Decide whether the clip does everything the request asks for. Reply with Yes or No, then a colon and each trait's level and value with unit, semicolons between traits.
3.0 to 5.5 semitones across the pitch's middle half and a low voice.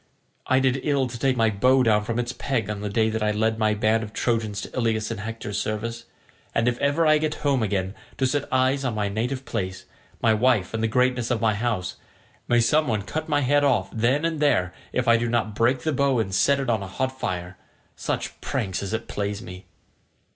Yes: average, 3.6 semitones; low, 115 Hz